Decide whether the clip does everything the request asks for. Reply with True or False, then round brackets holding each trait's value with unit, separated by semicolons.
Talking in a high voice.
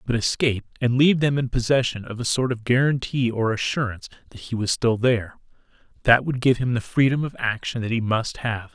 False (120 Hz)